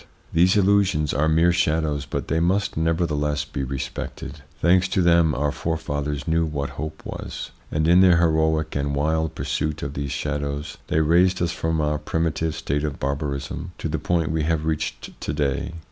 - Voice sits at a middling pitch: No, very low, 80 Hz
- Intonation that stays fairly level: Yes, narrow, 2.2 semitones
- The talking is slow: No, average, 175 wpm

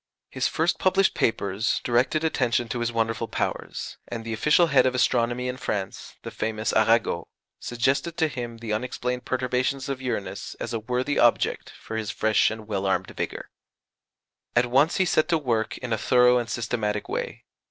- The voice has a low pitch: Yes, low, 120 Hz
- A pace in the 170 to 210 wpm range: Yes, average, 175 wpm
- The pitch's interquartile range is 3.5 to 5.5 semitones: No, narrow, 2.5 semitones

